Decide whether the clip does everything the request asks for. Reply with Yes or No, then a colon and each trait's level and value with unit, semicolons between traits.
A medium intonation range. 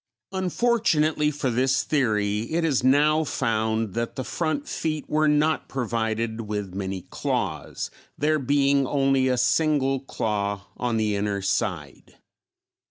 No: wide, 5.8 semitones